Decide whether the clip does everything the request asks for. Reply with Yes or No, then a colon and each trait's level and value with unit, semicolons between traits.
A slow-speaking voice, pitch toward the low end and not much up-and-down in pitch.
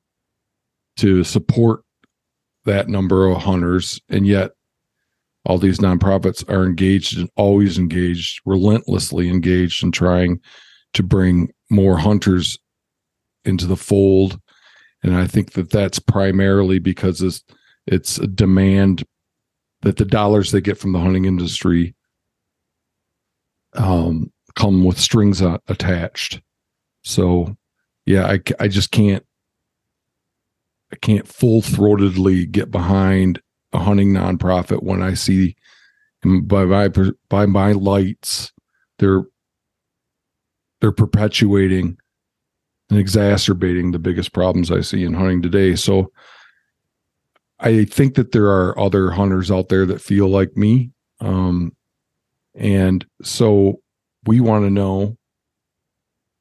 Yes: slow, 115 wpm; very low, 95 Hz; narrow, 1.9 semitones